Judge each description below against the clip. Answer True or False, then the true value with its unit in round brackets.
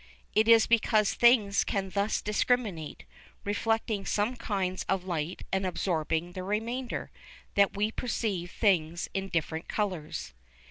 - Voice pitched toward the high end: True (200 Hz)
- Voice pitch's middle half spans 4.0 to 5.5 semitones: False (3.5 semitones)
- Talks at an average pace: False (130 wpm)